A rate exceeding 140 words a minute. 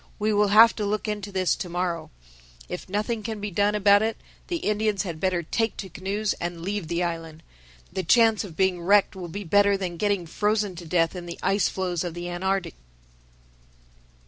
Yes: average, 200 wpm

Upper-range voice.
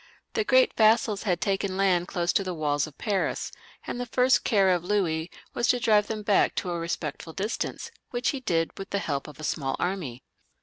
Yes: high, 195 Hz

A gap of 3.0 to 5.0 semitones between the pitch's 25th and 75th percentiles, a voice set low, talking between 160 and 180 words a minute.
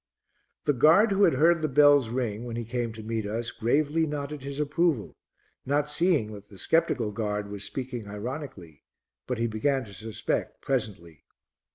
No: wide, 5.4 semitones; low, 125 Hz; average, 170 wpm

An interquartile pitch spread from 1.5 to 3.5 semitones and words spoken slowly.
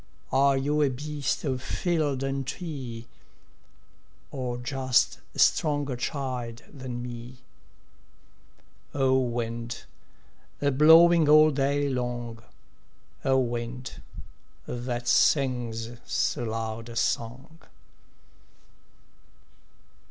Yes: average, 2.8 semitones; slow, 90 wpm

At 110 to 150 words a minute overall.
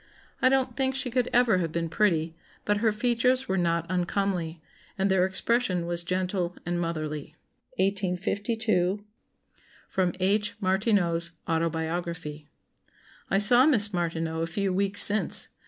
Yes: average, 140 wpm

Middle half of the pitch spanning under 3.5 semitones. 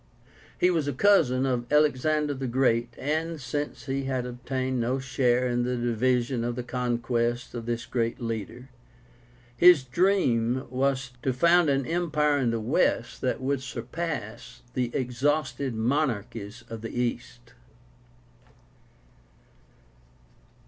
Yes: average, 2.9 semitones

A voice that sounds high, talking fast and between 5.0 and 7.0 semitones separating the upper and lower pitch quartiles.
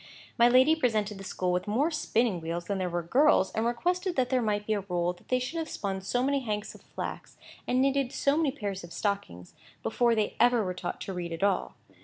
Yes: high, 215 Hz; fast, 235 wpm; wide, 5.4 semitones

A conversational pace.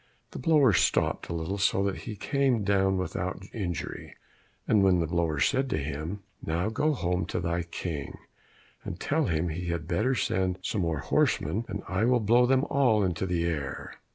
Yes: average, 185 wpm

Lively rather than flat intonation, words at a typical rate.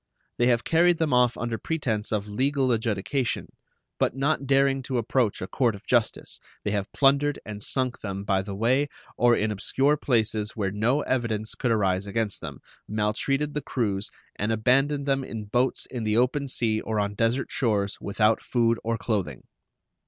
No: average, 4.2 semitones; average, 175 wpm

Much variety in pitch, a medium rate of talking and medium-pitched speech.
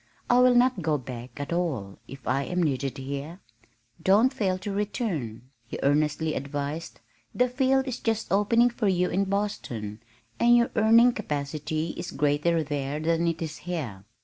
Yes: wide, 6.8 semitones; average, 165 wpm; medium, 165 Hz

